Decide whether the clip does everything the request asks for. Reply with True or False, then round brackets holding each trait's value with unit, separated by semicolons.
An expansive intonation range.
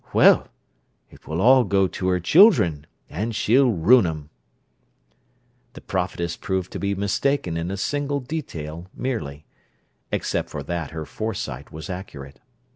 True (6.7 semitones)